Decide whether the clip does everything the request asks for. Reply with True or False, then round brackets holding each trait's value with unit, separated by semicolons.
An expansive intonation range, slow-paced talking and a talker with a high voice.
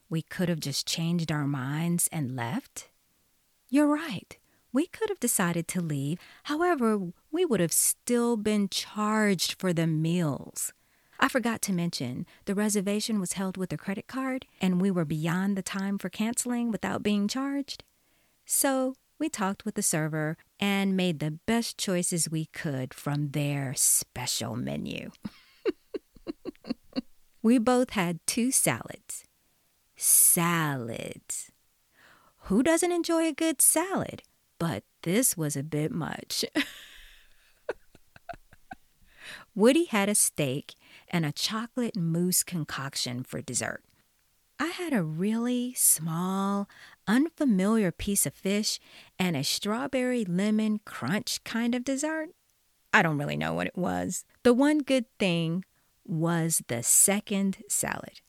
True (6.7 semitones; 130 wpm; 195 Hz)